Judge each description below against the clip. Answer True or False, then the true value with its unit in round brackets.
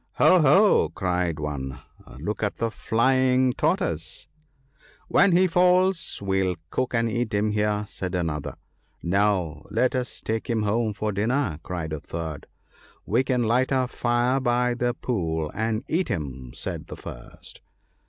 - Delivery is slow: False (170 wpm)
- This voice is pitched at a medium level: False (110 Hz)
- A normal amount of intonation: False (6.6 semitones)